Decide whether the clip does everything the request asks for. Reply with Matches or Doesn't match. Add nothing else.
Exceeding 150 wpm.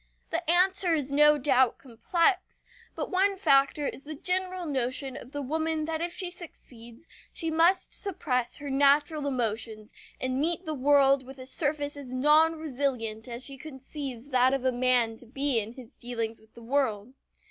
Matches